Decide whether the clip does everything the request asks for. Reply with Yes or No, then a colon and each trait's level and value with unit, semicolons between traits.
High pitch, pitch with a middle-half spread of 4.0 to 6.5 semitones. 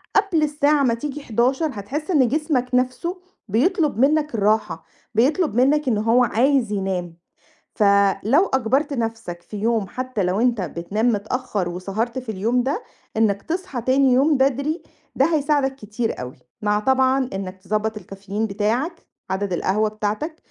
Yes: high, 240 Hz; average, 5.2 semitones